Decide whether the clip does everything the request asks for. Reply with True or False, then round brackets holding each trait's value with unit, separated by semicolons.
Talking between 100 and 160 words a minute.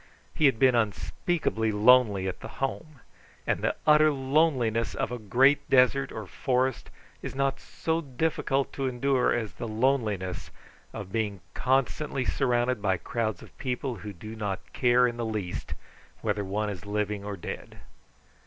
True (155 wpm)